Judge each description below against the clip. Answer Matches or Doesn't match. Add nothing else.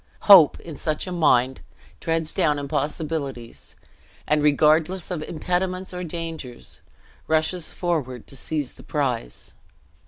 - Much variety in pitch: Doesn't match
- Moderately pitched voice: Matches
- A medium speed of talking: Doesn't match